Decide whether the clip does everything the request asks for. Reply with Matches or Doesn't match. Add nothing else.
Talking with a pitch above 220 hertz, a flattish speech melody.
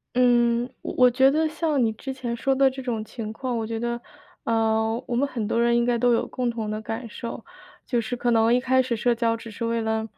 Matches